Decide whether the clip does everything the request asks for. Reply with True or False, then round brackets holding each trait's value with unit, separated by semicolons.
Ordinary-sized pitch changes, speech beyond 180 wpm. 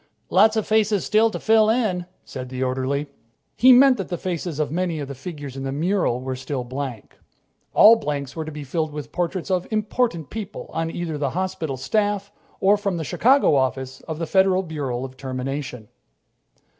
False (6.7 semitones; 190 wpm)